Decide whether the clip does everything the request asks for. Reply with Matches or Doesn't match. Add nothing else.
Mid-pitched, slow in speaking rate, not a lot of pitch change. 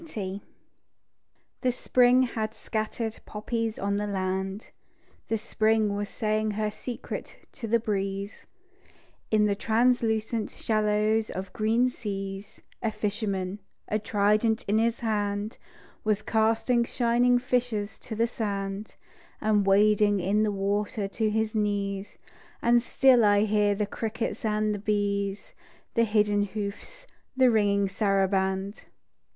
Doesn't match